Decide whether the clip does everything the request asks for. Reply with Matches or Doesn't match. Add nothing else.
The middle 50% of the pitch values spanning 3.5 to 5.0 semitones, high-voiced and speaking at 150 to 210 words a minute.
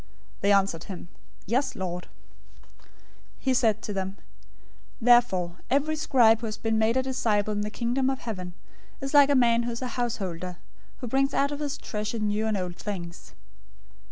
Matches